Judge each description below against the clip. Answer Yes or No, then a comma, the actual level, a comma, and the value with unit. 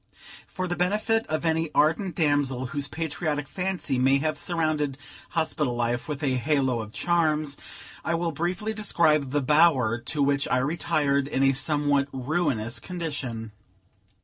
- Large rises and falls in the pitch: No, average, 3.6 semitones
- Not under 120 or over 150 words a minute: Yes, average, 145 wpm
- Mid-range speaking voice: Yes, medium, 150 Hz